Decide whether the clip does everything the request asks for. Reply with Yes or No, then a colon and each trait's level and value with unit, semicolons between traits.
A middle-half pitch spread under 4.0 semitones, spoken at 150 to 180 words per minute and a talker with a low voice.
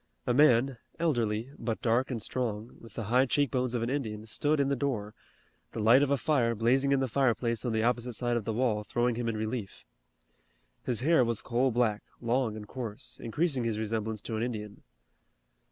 No: average, 2.8 semitones; average, 200 wpm; low, 120 Hz